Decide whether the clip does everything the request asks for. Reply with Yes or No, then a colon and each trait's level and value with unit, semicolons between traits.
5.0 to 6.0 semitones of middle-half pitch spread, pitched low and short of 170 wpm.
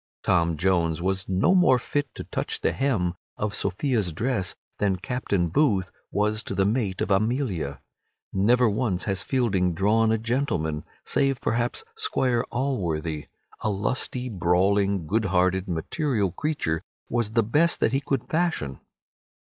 Yes: wide, 5.4 semitones; low, 105 Hz; average, 150 wpm